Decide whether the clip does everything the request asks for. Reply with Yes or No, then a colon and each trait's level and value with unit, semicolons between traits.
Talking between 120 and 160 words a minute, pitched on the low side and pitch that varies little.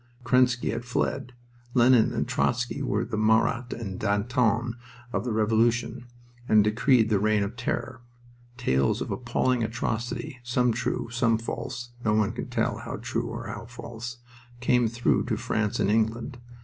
Yes: average, 155 wpm; low, 115 Hz; narrow, 2.1 semitones